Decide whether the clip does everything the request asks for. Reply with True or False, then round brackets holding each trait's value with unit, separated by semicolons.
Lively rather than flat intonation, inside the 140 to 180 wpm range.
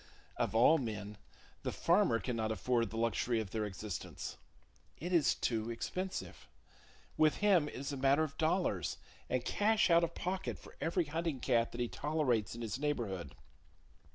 True (6.1 semitones; 165 wpm)